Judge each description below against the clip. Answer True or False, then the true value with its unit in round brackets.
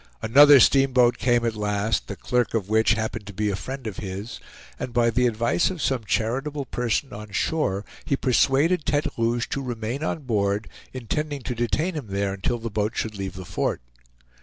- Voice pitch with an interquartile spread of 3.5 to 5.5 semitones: True (4.1 semitones)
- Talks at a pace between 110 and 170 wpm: False (190 wpm)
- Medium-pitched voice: False (115 Hz)